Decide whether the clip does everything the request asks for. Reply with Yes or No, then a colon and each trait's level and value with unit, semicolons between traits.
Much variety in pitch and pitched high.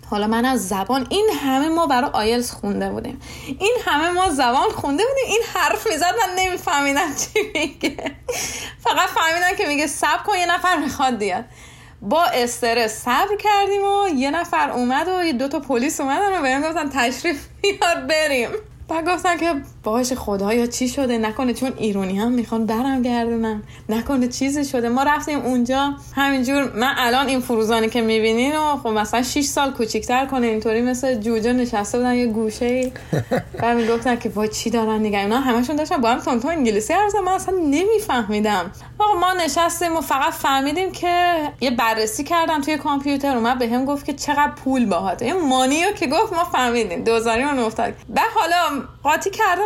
Yes: wide, 6.0 semitones; very high, 275 Hz